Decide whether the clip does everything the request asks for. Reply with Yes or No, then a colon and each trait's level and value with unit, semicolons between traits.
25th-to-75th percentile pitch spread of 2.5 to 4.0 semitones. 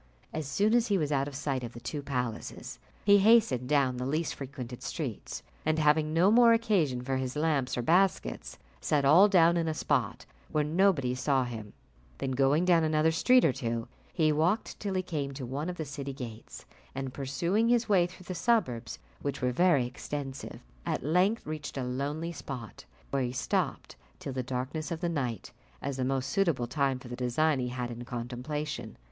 No: average, 4.8 semitones